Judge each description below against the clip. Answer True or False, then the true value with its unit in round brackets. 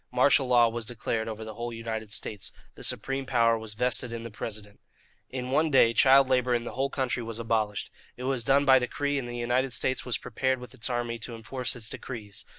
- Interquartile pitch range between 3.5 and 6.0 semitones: False (2.5 semitones)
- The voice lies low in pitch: True (120 Hz)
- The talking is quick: True (220 wpm)